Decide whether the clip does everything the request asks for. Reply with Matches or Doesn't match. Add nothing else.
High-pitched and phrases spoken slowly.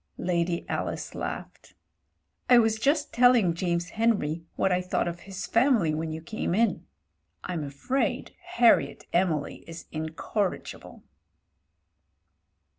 Doesn't match